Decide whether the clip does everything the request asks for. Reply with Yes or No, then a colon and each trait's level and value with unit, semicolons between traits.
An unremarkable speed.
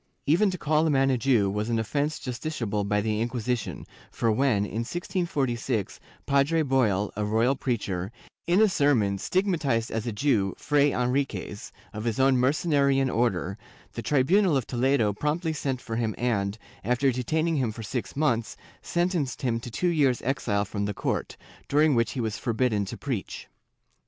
Yes: average, 170 wpm